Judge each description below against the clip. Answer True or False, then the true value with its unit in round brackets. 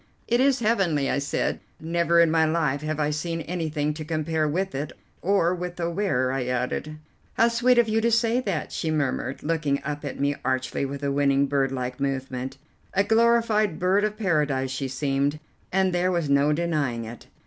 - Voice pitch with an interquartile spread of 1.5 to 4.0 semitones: False (4.9 semitones)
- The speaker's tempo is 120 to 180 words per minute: False (190 wpm)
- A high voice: False (155 Hz)